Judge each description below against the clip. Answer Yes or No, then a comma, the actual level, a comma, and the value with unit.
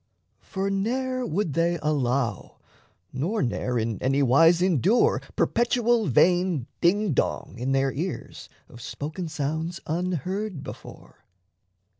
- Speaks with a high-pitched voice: No, medium, 165 Hz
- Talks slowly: Yes, slow, 105 wpm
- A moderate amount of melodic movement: No, wide, 6.2 semitones